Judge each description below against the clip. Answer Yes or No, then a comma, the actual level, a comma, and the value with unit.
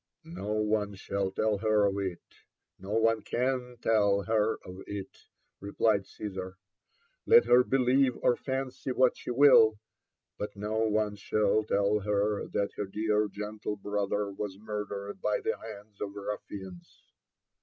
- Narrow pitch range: Yes, narrow, 1.8 semitones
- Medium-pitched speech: No, low, 105 Hz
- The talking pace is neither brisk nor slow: Yes, average, 150 wpm